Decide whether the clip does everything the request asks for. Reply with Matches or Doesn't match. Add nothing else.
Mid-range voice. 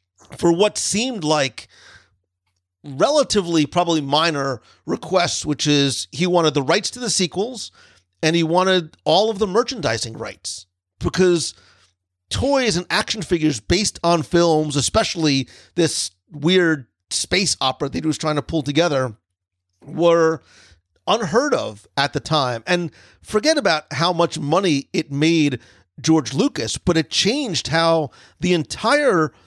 Matches